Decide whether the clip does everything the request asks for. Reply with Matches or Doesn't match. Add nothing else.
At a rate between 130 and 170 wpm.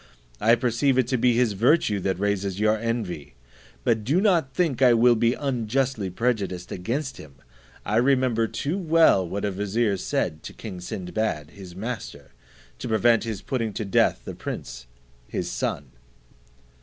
Matches